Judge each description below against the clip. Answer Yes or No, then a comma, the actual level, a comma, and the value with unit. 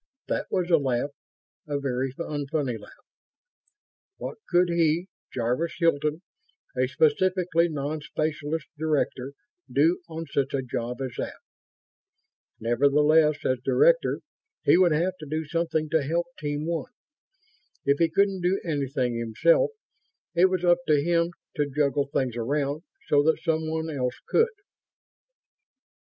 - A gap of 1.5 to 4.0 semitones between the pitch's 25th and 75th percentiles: Yes, average, 3.3 semitones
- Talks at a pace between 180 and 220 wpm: No, slow, 135 wpm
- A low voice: No, medium, 155 Hz